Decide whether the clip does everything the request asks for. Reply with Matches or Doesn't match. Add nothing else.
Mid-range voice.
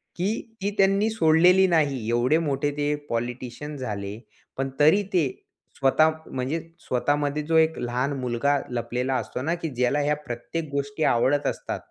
Matches